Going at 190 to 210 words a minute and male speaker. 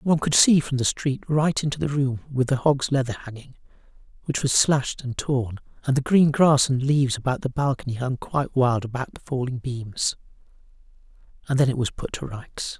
Yes: average, 200 wpm; male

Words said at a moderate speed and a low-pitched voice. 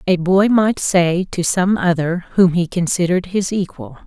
No: average, 175 wpm; medium, 180 Hz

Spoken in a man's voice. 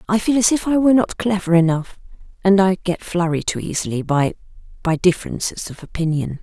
No: female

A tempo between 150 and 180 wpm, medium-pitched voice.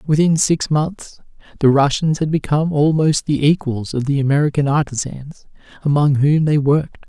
Yes: average, 155 wpm; medium, 145 Hz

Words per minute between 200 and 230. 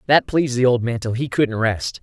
No: fast, 265 wpm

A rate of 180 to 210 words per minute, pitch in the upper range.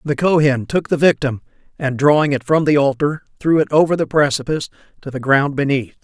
No: average, 200 wpm; medium, 145 Hz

